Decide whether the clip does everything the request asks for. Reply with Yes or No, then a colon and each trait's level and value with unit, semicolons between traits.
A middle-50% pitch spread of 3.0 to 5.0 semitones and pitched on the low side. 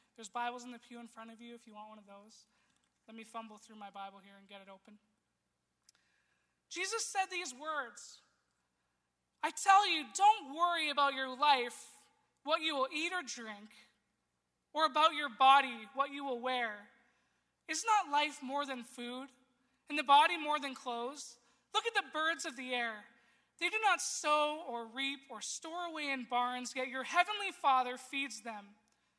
No: average, 4.6 semitones; very high, 270 Hz